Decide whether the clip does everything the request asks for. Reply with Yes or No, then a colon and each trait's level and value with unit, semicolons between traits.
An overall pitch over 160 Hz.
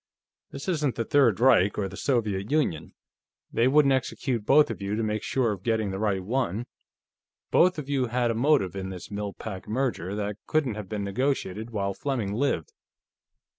No: low, 110 Hz